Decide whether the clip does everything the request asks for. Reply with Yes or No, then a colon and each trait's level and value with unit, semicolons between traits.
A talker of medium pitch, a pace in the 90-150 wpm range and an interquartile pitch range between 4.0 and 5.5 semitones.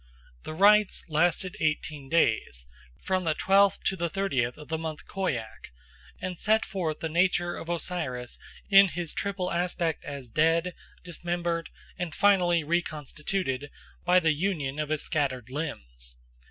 No: medium, 165 Hz; average, 140 wpm; average, 3.6 semitones